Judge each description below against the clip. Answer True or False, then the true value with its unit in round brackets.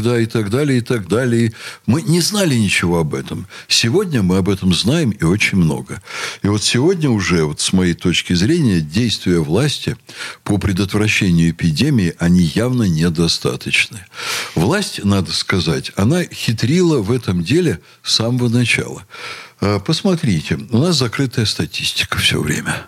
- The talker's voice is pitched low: True (110 Hz)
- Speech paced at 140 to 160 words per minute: True (145 wpm)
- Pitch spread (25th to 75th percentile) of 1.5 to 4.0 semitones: False (5.5 semitones)